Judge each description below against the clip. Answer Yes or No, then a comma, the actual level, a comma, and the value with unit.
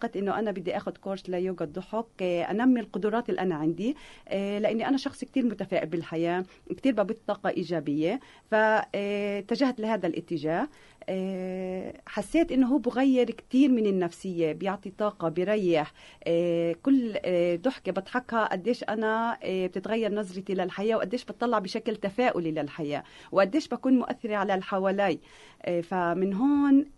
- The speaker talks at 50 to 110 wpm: No, average, 120 wpm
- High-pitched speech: Yes, high, 200 Hz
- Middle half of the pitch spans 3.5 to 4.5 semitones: Yes, average, 4.2 semitones